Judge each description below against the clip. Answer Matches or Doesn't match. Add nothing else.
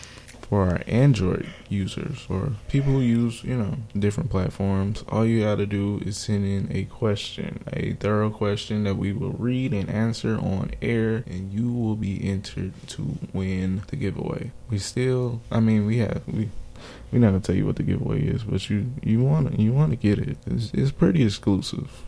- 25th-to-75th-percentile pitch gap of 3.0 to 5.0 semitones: Matches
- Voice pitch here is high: Doesn't match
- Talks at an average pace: Matches